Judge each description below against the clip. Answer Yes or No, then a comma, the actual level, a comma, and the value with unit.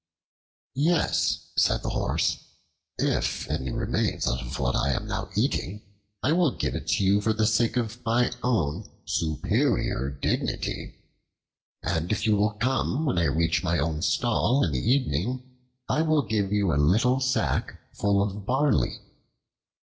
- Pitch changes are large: Yes, wide, 7.1 semitones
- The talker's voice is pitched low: Yes, low, 105 Hz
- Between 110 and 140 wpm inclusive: No, average, 155 wpm